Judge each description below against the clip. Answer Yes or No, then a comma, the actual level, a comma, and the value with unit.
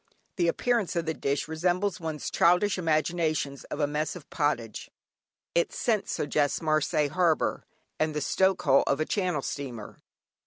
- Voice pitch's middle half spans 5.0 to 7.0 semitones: No, average, 3.4 semitones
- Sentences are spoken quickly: No, average, 155 wpm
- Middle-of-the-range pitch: Yes, medium, 155 Hz